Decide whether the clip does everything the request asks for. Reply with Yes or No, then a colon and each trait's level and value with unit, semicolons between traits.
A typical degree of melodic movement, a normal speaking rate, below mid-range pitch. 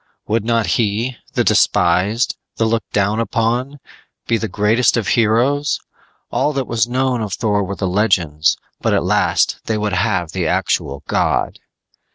Yes: average, 3.0 semitones; average, 160 wpm; low, 110 Hz